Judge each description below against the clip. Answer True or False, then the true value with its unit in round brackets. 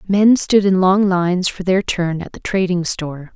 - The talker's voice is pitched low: False (185 Hz)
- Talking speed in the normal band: False (215 wpm)